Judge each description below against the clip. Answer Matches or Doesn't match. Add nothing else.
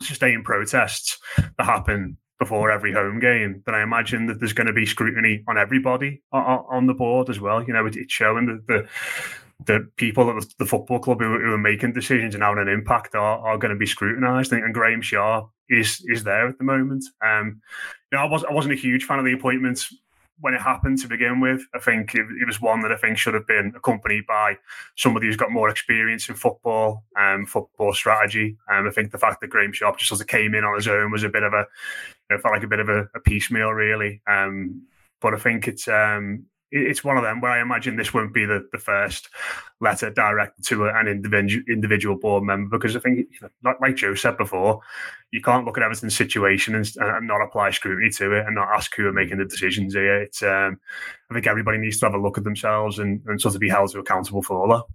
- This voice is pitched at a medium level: Doesn't match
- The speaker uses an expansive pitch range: Doesn't match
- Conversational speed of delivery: Doesn't match